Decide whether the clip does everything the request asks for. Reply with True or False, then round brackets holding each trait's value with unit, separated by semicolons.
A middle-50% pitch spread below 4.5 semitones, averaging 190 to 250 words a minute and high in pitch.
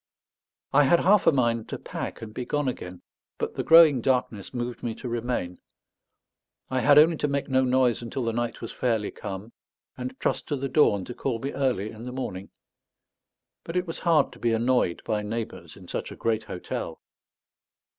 False (3.6 semitones; 195 wpm; 125 Hz)